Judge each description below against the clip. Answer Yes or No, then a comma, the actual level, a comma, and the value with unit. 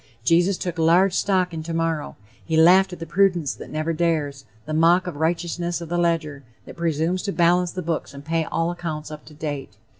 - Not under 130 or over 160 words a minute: No, average, 200 wpm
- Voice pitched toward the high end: No, medium, 165 Hz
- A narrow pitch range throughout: Yes, narrow, 2.0 semitones